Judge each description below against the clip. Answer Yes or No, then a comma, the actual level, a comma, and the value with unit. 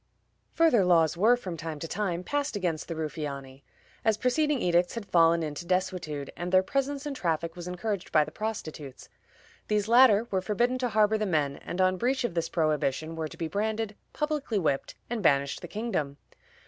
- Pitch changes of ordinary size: No, wide, 5.7 semitones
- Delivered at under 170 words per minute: No, average, 185 wpm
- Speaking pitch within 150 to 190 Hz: Yes, medium, 185 Hz